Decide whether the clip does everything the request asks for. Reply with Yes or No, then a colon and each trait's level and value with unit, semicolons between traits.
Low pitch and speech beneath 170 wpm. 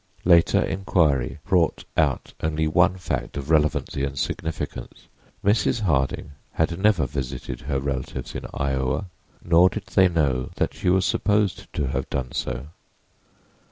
Yes: very low, 80 Hz; average, 140 wpm